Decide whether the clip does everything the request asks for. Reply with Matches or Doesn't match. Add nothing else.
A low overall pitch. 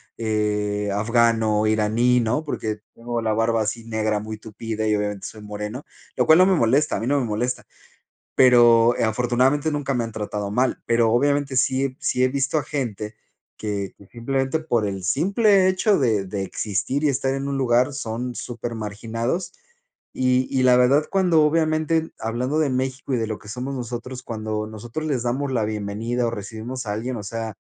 Matches